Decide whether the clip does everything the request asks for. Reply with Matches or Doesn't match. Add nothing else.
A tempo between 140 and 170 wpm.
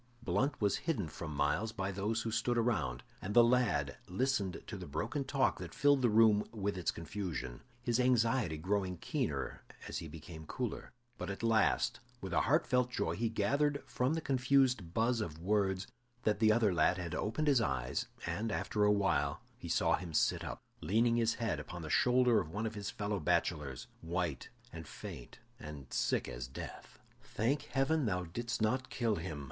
Doesn't match